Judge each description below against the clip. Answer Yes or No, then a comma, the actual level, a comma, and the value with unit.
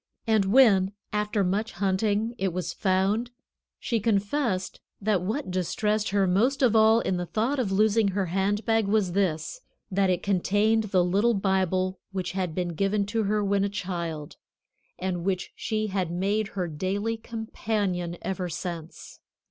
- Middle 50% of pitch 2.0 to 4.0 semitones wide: Yes, average, 2.8 semitones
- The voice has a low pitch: No, high, 195 Hz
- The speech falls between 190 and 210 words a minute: No, average, 160 wpm